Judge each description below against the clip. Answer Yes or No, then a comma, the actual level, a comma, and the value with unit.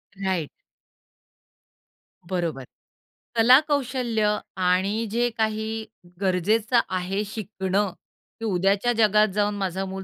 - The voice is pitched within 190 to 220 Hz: Yes, high, 210 Hz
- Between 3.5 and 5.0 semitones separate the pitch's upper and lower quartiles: No, average, 2.9 semitones